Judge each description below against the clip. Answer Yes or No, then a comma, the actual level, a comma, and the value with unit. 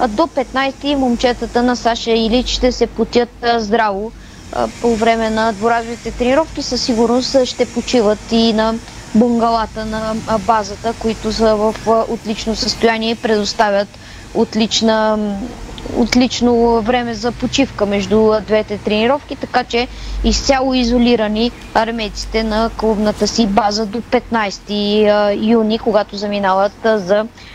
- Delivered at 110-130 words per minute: Yes, average, 120 wpm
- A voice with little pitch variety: Yes, narrow, 1.7 semitones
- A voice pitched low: No, high, 230 Hz